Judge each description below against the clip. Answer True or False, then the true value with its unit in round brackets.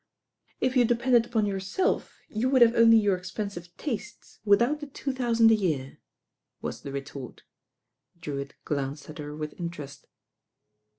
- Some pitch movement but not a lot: False (7.8 semitones)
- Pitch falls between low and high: False (205 Hz)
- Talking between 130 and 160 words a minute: True (150 wpm)